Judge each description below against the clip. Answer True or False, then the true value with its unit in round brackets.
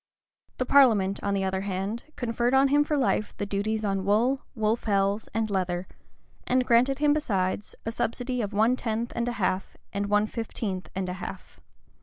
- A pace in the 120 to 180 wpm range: False (190 wpm)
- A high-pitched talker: True (220 Hz)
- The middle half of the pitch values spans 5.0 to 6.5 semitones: False (3.6 semitones)